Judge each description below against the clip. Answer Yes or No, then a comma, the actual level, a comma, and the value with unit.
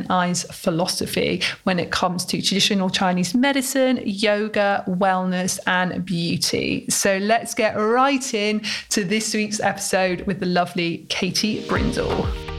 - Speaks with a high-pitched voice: Yes, high, 195 Hz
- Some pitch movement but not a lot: Yes, average, 3.1 semitones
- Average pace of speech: No, slow, 130 wpm